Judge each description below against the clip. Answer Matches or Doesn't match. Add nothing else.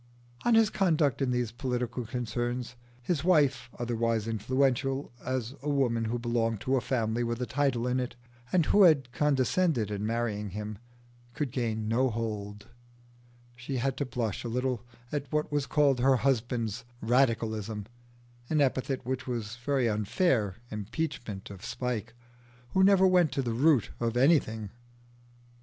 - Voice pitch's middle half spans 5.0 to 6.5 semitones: Doesn't match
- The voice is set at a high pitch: Doesn't match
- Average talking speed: Matches